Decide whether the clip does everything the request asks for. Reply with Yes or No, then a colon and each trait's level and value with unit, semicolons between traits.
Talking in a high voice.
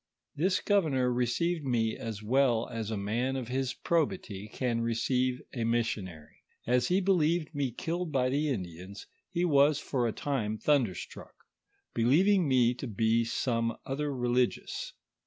No: low, 125 Hz